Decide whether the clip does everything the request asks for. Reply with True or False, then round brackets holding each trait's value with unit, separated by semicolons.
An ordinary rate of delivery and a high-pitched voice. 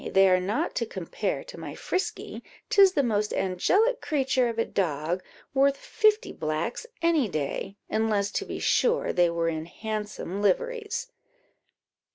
True (150 wpm; 220 Hz)